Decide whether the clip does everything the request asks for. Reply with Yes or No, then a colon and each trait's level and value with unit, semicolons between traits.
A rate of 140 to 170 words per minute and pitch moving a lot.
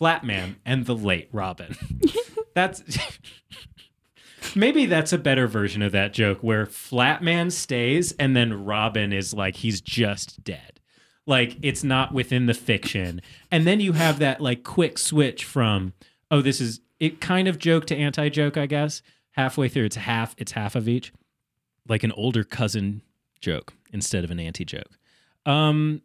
Yes: average, 165 wpm; wide, 6.0 semitones